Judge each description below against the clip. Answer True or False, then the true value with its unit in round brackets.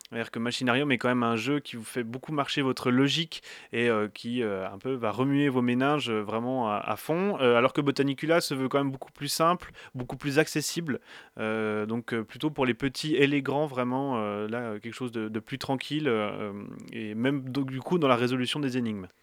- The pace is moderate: False (230 wpm)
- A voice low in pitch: True (130 Hz)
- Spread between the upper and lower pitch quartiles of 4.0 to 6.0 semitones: False (3.4 semitones)